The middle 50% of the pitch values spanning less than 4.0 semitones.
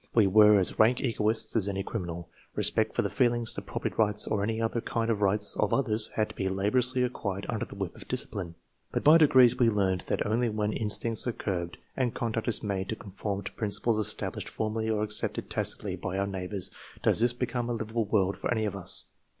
Yes: average, 2.7 semitones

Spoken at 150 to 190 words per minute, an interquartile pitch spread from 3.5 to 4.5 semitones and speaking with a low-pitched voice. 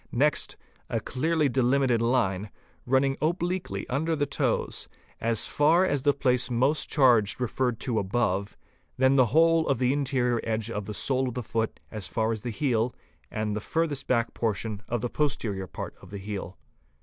Yes: average, 185 wpm; average, 4.1 semitones; low, 125 Hz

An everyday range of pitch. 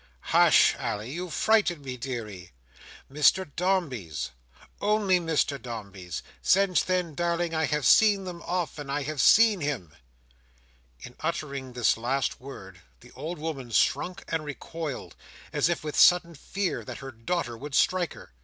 No: wide, 6.1 semitones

